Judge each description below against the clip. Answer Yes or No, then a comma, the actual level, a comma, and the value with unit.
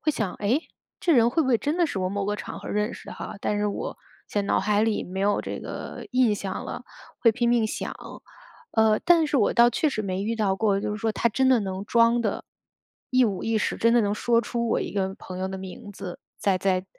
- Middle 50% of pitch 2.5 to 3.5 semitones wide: Yes, average, 3.1 semitones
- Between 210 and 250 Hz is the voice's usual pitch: Yes, high, 215 Hz